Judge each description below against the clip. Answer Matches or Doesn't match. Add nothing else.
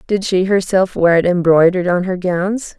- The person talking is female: Matches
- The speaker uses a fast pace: Doesn't match